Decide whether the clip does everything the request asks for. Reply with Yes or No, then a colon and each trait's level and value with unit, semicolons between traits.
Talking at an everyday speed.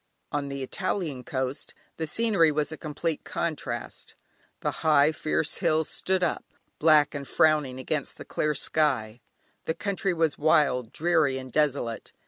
Yes: average, 145 wpm